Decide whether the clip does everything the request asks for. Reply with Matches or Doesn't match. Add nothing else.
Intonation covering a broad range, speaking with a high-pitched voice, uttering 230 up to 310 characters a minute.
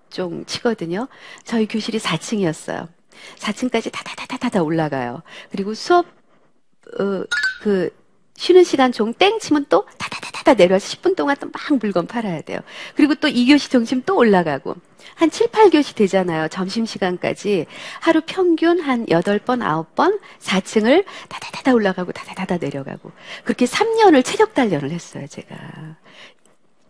Matches